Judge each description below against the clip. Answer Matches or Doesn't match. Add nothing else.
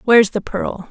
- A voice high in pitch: Matches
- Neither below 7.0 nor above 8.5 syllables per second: Doesn't match